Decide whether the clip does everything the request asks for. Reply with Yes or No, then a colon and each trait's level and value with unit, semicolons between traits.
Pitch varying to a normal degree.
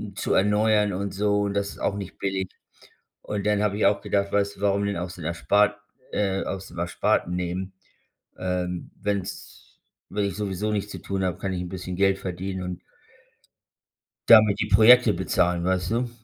No: narrow, 2.0 semitones